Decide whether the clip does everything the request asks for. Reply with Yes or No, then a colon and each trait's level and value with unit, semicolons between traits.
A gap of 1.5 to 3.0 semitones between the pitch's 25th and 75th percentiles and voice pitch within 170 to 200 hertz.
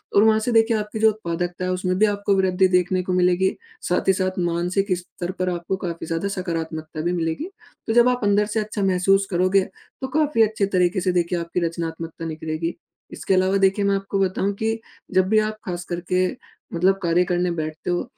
Yes: narrow, 2.5 semitones; medium, 185 Hz